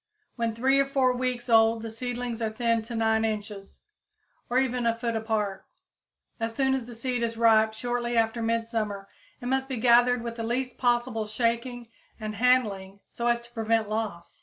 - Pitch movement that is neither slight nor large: No, narrow, 1.8 semitones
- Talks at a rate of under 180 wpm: No, average, 185 wpm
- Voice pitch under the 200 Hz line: No, high, 230 Hz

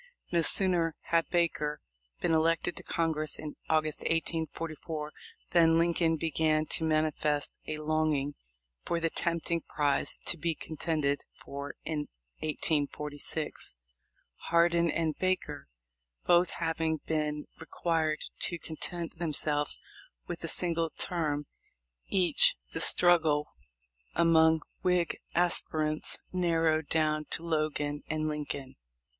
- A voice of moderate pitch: Yes, medium, 160 Hz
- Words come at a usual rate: No, slow, 110 wpm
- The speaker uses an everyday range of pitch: No, narrow, 1.7 semitones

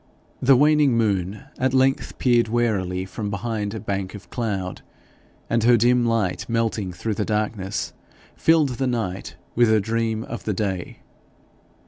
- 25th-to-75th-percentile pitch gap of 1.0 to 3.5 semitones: Yes, average, 3.1 semitones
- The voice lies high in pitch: No, low, 110 Hz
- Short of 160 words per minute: Yes, average, 150 wpm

